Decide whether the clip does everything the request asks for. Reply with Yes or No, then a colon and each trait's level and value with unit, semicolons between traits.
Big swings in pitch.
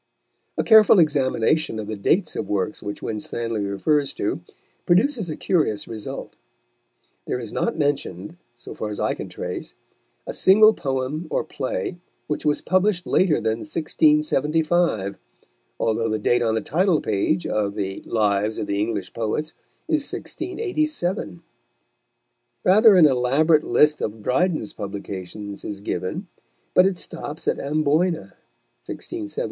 Yes: wide, 8.4 semitones